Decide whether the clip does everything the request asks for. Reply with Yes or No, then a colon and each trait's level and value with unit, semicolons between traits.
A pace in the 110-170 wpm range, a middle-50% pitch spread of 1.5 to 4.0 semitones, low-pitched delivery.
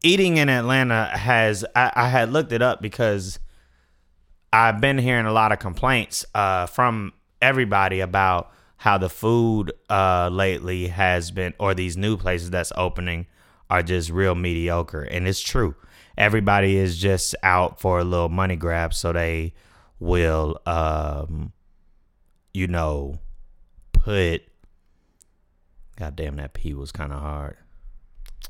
Yes: average, 140 wpm; average, 3.7 semitones; very low, 90 Hz